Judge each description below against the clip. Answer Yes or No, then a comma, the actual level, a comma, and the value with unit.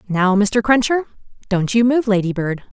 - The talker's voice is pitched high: Yes, high, 215 Hz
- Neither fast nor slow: No, slow, 130 wpm